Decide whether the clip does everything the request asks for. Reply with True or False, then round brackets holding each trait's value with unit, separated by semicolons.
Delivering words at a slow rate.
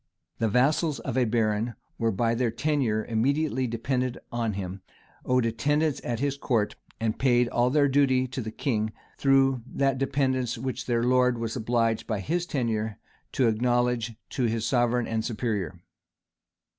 False (155 wpm)